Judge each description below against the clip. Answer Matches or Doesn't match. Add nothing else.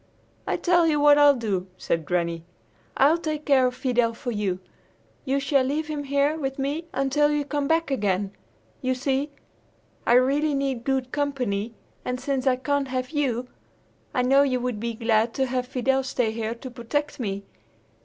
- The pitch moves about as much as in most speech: Matches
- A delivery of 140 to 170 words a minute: Doesn't match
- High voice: Matches